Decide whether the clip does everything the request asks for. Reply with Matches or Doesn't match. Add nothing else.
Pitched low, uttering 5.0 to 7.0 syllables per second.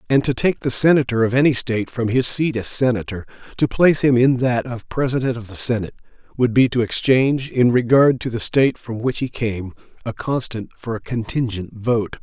Matches